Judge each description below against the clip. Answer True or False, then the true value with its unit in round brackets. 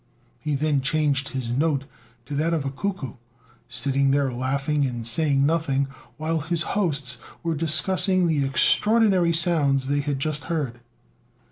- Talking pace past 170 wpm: False (145 wpm)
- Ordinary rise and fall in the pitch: True (3.2 semitones)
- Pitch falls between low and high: True (145 Hz)